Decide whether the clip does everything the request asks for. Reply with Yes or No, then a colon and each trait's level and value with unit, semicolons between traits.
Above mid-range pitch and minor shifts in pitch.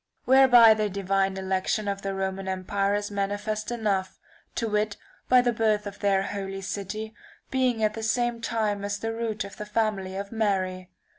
Yes: high, 205 Hz; narrow, 2.2 semitones